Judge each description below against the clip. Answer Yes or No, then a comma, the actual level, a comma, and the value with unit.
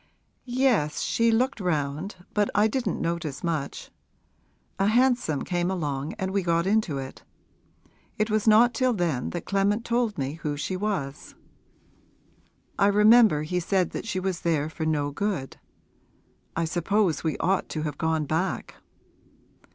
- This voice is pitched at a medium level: Yes, medium, 180 Hz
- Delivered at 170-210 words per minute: No, average, 150 wpm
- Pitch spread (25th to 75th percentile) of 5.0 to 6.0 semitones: Yes, wide, 5.4 semitones